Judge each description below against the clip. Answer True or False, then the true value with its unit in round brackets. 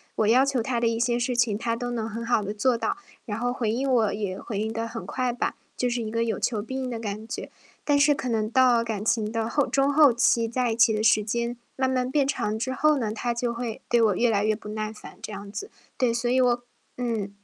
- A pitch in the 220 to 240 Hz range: True (235 Hz)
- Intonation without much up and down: True (2.3 semitones)